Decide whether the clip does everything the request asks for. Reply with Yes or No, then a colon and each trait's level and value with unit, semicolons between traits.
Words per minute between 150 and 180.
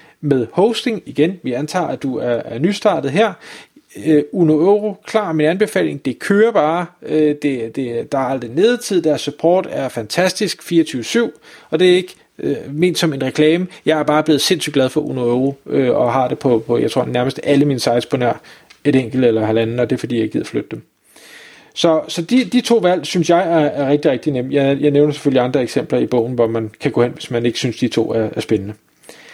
No: fast, 225 wpm